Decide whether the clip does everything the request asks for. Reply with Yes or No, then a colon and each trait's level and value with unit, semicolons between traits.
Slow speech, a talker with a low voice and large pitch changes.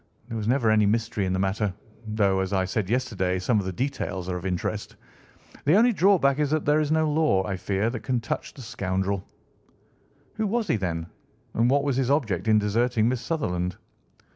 No: fast, 205 wpm; low, 110 Hz; wide, 6.5 semitones